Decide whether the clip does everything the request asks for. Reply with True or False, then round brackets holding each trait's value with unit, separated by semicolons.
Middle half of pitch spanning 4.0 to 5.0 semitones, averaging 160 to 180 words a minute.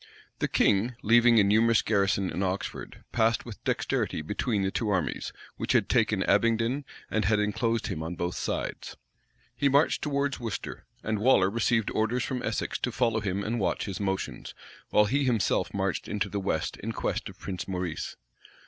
False (3.2 semitones; 175 wpm)